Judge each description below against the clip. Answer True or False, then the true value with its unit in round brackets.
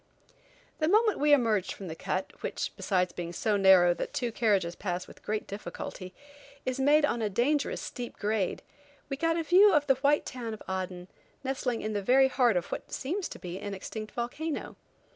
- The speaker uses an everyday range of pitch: False (6.7 semitones)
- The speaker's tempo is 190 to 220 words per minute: True (195 wpm)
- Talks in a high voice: True (230 Hz)